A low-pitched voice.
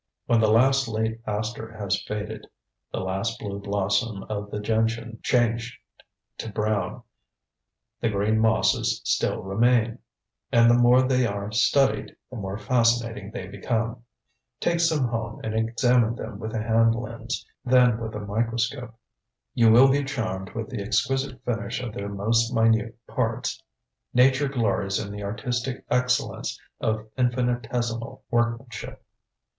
Yes: low, 115 Hz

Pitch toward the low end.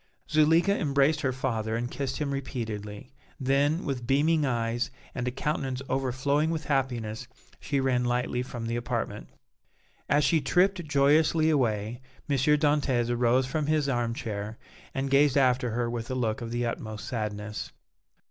Yes: low, 130 Hz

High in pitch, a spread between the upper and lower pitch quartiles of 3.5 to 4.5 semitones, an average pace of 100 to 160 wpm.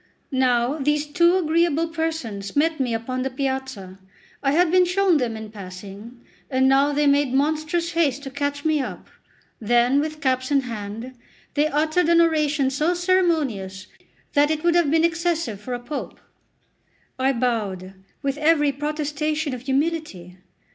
Yes: very high, 285 Hz; average, 4.2 semitones; average, 155 wpm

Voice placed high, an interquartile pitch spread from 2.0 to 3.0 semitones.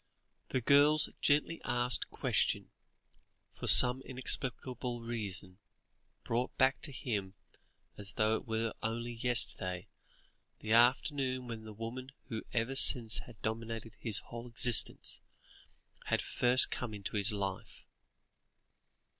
No: low, 115 Hz; narrow, 2.5 semitones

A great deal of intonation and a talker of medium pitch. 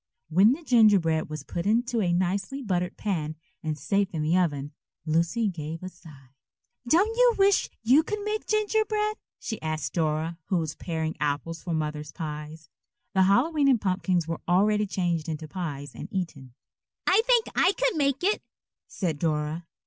Yes: wide, 7.4 semitones; medium, 180 Hz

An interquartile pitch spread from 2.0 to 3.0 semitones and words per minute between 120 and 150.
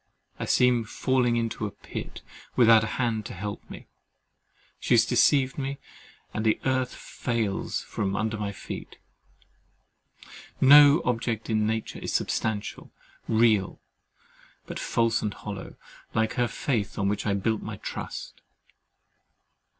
Yes: average, 2.7 semitones; slow, 135 wpm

